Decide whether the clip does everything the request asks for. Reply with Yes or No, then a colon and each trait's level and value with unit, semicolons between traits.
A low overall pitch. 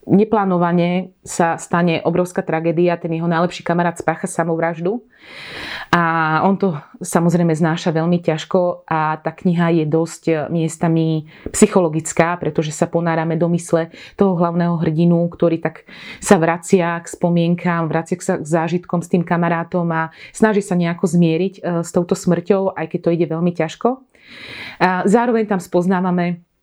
No: medium, 170 Hz